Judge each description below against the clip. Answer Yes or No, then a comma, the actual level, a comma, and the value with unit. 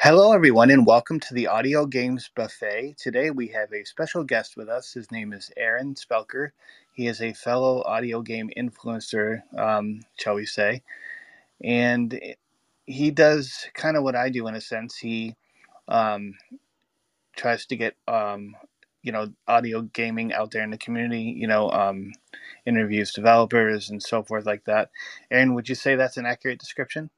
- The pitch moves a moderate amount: Yes, average, 3.2 semitones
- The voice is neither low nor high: No, low, 115 Hz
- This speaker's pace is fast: No, average, 170 wpm